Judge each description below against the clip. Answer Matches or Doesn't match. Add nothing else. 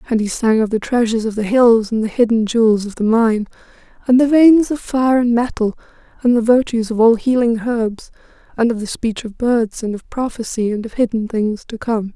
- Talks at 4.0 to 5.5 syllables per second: Matches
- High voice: Matches